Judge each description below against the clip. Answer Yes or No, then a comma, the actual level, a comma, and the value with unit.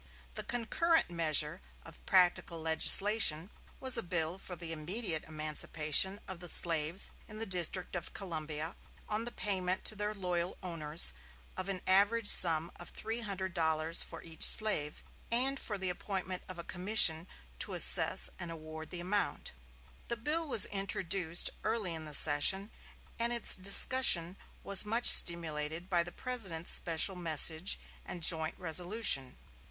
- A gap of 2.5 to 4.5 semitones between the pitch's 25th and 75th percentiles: Yes, average, 4.1 semitones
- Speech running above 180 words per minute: No, average, 150 wpm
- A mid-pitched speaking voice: Yes, medium, 180 Hz